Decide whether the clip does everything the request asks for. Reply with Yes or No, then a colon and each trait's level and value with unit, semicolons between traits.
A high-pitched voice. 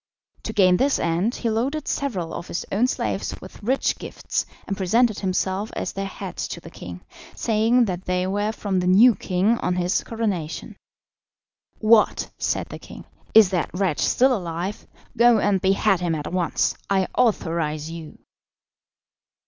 Yes: high, 195 Hz